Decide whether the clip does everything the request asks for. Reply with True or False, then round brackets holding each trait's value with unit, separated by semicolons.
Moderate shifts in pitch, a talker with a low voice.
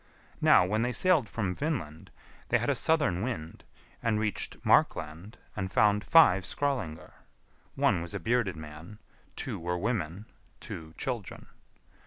False (6.0 semitones; 105 Hz)